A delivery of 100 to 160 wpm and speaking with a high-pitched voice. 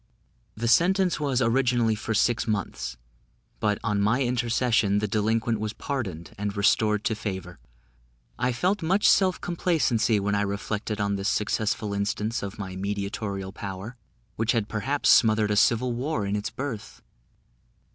No: average, 150 wpm; low, 110 Hz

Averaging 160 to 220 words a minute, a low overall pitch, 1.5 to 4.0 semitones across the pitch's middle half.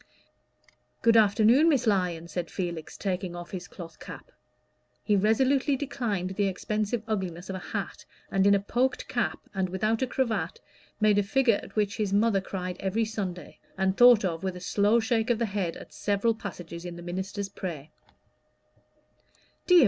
No: average, 170 wpm; high, 200 Hz; average, 3.6 semitones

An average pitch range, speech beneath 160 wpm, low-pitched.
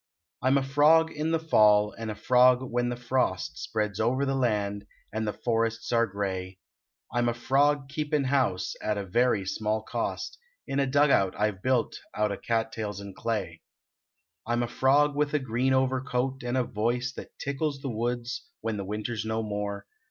No: average, 3.9 semitones; average, 200 wpm; low, 120 Hz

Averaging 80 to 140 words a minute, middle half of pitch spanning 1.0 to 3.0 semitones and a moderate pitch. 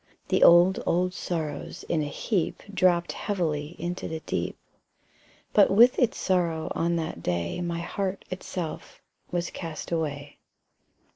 Yes: slow, 135 wpm; narrow, 2.5 semitones; medium, 170 Hz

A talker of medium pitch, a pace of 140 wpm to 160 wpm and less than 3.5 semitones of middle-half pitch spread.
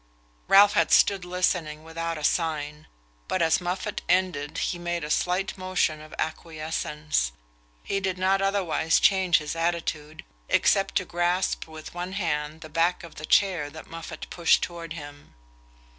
Yes: medium, 165 Hz; average, 155 wpm; average, 2.9 semitones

